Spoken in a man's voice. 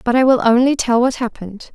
No: female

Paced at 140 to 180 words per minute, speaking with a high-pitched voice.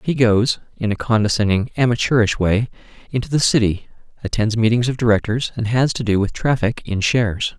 No: average, 175 wpm; low, 115 Hz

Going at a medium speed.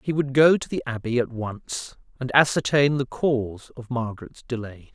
Yes: average, 180 wpm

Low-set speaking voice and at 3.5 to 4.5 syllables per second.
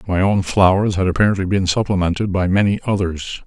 No: very low, 95 Hz; 5.9 syllables/s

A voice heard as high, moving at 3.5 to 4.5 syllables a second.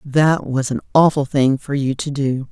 No: medium, 140 Hz; 4.4 syllables/s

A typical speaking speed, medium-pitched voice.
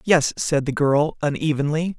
Yes: average, 150 wpm; medium, 150 Hz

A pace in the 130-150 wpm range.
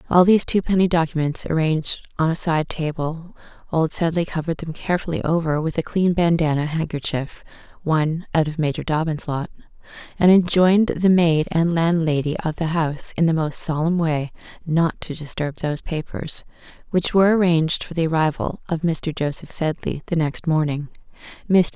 No: average, 165 wpm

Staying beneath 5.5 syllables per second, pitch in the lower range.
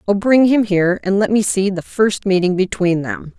No: 5.0 syllables/s; high, 200 Hz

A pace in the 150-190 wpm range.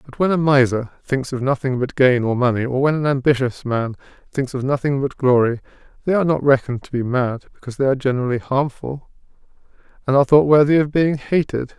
No: fast, 205 wpm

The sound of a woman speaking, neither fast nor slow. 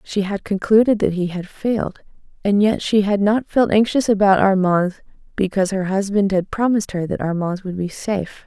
Yes: female; average, 190 wpm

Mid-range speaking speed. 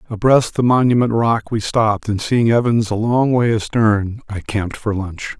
Yes: average, 190 wpm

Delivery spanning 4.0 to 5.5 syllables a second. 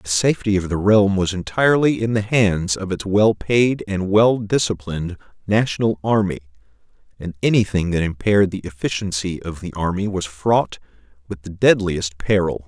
Yes: 5.1 syllables/s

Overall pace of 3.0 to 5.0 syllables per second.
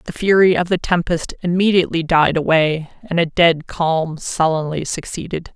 Yes: 4.7 syllables/s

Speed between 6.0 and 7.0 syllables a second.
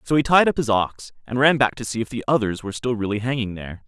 Yes: 6.6 syllables/s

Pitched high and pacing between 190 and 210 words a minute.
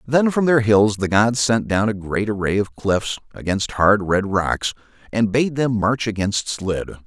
No: low, 110 Hz; average, 195 wpm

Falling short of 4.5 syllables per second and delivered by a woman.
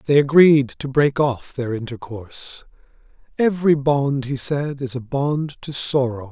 No: 4.3 syllables/s; male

